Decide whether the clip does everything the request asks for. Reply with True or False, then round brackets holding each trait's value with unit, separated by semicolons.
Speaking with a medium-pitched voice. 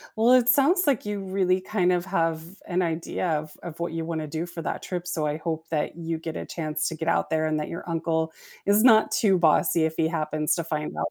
True (165 Hz)